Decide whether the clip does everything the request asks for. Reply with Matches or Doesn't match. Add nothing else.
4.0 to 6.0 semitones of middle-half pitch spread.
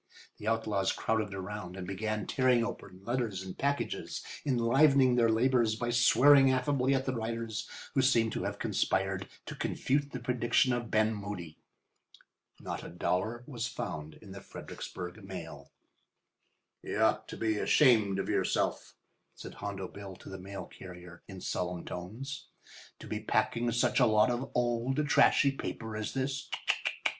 Matches